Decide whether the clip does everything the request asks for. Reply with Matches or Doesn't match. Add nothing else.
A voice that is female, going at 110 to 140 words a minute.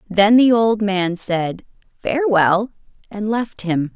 Matches